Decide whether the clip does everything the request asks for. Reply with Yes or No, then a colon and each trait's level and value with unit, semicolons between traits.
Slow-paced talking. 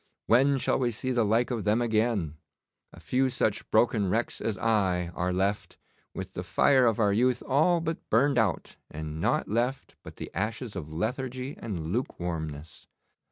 No: average, 165 wpm